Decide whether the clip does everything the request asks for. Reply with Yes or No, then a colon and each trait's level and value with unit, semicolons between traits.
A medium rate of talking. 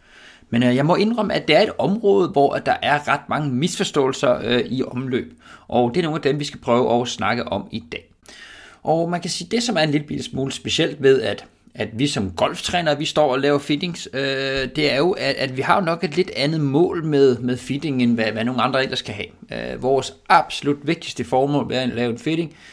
No: fast, 240 wpm